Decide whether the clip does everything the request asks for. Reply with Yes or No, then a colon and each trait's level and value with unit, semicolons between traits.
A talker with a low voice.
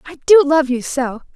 No: very high, 285 Hz